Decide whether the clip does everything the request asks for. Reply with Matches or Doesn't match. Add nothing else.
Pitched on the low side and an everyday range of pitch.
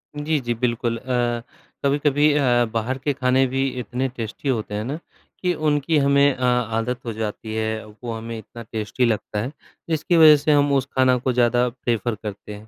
Matches